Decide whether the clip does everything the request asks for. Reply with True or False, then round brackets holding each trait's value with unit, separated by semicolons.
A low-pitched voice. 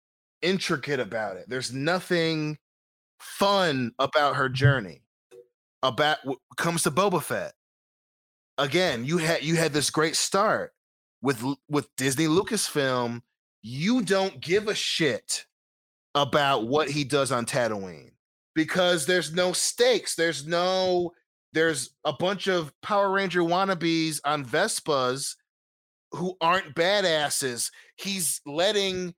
False (155 Hz)